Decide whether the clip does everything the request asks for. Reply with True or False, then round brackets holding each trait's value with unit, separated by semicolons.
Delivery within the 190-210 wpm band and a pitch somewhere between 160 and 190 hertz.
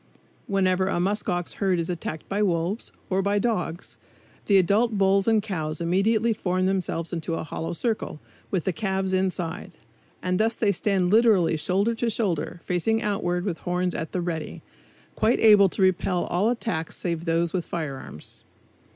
False (170 wpm; 185 Hz)